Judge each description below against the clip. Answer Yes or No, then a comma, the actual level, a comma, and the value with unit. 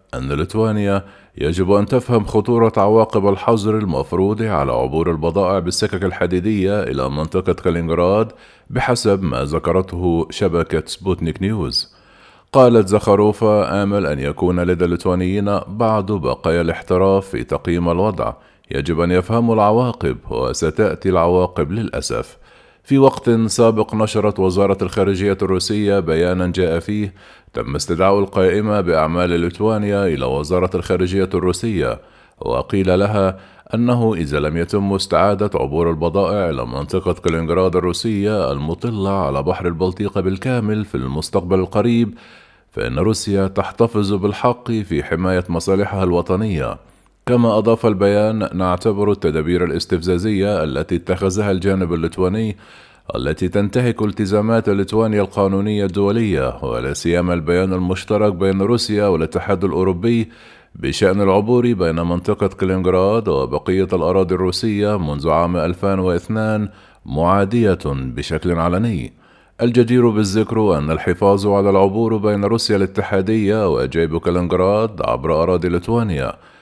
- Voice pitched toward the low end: Yes, very low, 95 Hz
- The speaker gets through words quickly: No, average, 110 wpm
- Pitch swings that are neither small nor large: Yes, average, 3.1 semitones